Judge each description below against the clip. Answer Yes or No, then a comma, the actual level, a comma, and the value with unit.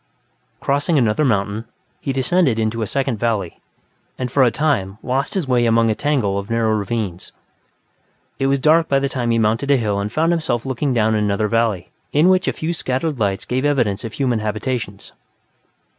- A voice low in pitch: Yes, low, 120 Hz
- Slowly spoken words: No, average, 190 wpm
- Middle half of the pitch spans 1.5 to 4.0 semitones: No, average, 4.4 semitones